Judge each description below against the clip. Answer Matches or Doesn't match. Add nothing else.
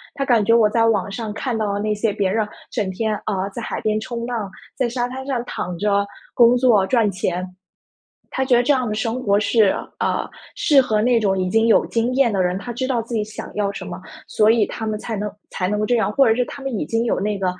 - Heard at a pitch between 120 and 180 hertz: Doesn't match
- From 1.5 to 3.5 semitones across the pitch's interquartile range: Matches